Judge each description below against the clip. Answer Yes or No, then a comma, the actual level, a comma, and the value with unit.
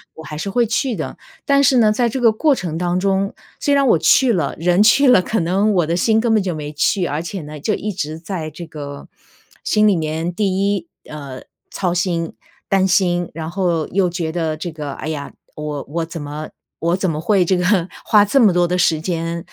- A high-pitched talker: No, medium, 175 Hz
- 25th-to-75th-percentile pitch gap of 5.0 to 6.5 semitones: No, average, 4.3 semitones